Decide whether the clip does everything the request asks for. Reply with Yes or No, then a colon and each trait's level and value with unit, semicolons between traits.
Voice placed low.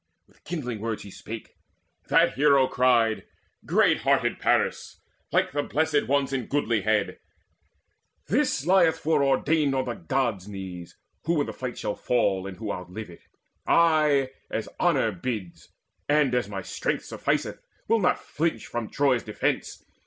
Yes: low, 125 Hz